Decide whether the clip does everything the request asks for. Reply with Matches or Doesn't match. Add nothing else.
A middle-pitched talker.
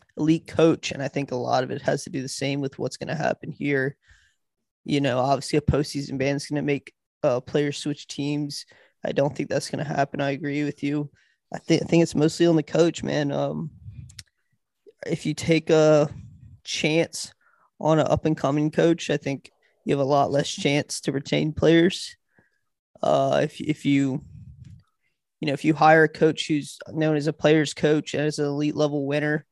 Matches